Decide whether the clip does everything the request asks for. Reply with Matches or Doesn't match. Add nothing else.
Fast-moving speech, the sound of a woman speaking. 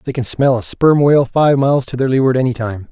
Doesn't match